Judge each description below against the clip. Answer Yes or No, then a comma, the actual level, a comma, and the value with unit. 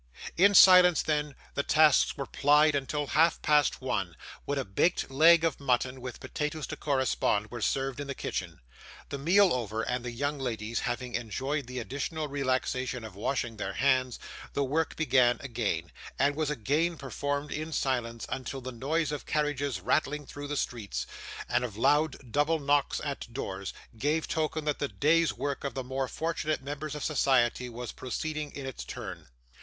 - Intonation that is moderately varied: Yes, average, 3.3 semitones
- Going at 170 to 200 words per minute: Yes, average, 175 wpm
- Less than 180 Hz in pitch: Yes, medium, 140 Hz